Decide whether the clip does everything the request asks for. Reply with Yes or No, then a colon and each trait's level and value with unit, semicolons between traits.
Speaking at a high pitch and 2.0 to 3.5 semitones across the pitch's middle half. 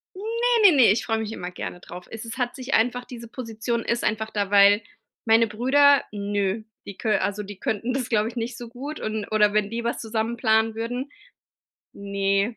Yes: high, 225 Hz; average, 2.9 semitones